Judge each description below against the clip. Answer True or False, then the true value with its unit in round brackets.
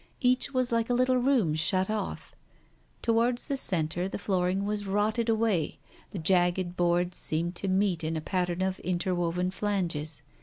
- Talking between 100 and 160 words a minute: False (175 wpm)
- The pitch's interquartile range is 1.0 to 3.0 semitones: False (4.1 semitones)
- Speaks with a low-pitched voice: False (190 Hz)